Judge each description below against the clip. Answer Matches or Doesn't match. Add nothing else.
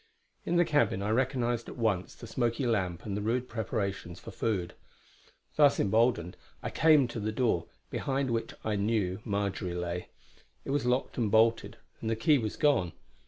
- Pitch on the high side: Doesn't match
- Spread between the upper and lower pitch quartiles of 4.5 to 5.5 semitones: Doesn't match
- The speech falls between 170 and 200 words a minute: Matches